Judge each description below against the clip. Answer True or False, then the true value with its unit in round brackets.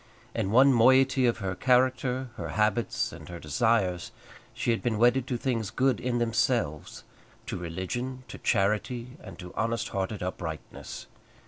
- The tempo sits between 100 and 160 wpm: True (150 wpm)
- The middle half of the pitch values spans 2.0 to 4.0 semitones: False (4.6 semitones)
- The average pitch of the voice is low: True (115 Hz)